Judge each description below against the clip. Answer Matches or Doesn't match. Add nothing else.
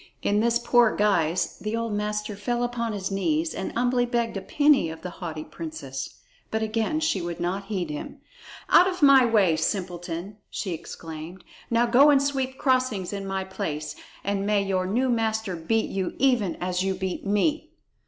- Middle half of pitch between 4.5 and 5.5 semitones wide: Matches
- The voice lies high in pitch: Matches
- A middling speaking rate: Matches